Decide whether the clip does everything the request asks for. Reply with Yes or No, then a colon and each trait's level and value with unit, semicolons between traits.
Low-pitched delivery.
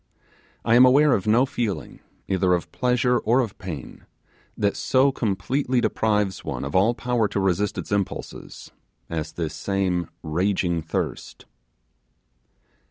Yes: low, 100 Hz